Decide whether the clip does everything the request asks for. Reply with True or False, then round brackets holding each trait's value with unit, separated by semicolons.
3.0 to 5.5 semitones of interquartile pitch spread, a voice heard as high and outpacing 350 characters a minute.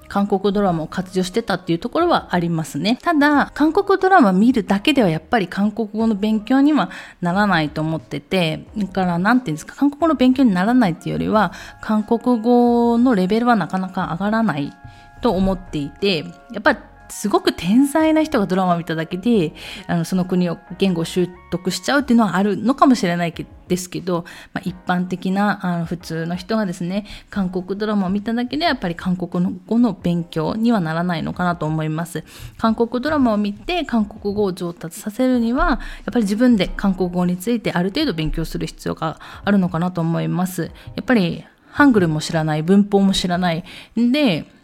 True (5.2 semitones; 195 Hz; 390 characters per minute)